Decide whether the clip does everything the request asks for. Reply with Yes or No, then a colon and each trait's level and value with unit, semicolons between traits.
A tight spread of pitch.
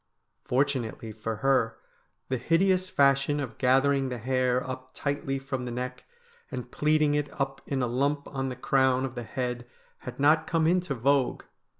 Yes: narrow, 2.2 semitones